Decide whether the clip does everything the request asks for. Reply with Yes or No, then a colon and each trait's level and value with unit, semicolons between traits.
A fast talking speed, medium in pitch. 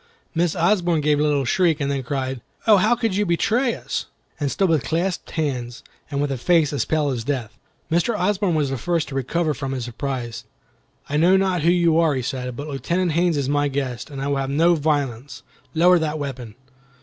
Yes: fast, 210 wpm; medium, 150 Hz